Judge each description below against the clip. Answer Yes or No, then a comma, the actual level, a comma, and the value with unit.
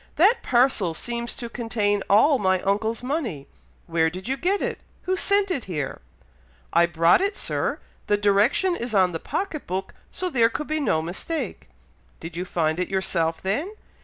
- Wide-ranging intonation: Yes, wide, 8.5 semitones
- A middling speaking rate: Yes, average, 175 wpm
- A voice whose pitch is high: Yes, high, 215 Hz